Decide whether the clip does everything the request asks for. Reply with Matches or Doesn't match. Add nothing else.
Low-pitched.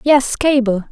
Doesn't match